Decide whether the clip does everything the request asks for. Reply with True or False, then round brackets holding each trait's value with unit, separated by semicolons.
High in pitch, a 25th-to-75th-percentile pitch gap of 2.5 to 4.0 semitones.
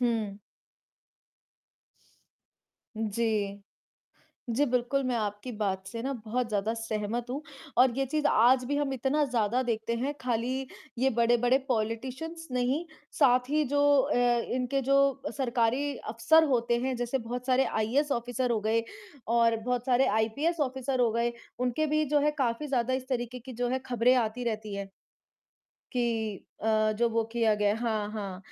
True (245 Hz; 2.9 semitones)